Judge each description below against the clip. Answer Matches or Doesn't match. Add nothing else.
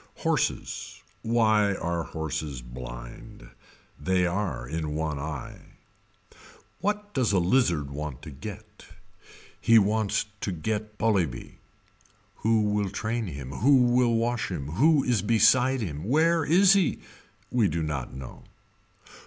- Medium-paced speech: Doesn't match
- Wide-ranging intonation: Matches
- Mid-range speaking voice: Doesn't match